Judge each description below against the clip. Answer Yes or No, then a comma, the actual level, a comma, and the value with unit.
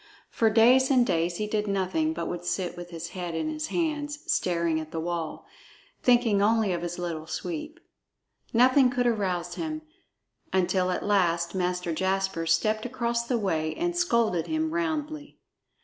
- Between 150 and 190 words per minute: Yes, average, 165 wpm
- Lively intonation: Yes, wide, 6.9 semitones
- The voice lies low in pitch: No, high, 205 Hz